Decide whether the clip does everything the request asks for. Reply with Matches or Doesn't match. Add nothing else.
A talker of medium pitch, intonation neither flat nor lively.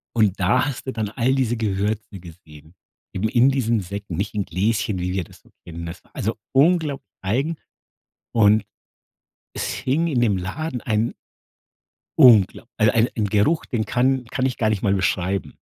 Doesn't match